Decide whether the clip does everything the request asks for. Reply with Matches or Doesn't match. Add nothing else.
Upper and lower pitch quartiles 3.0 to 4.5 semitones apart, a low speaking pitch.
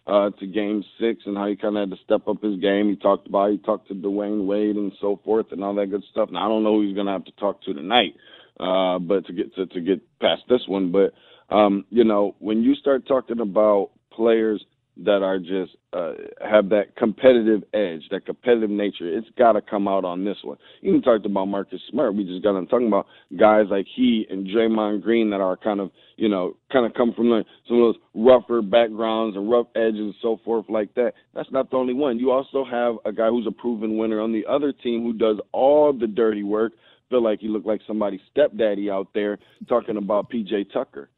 Doesn't match